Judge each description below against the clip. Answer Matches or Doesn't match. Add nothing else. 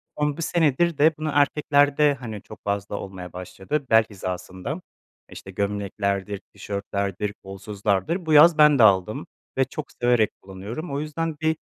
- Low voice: Matches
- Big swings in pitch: Matches